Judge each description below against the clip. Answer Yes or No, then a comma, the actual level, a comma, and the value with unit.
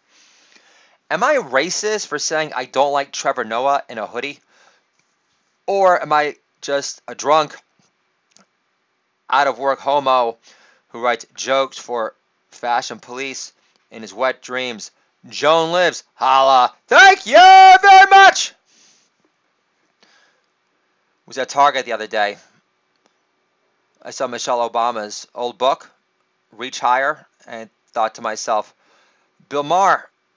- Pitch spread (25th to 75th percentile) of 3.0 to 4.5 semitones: No, average, 5.1 semitones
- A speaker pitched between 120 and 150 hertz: Yes, low, 135 Hz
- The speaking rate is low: Yes, slow, 120 wpm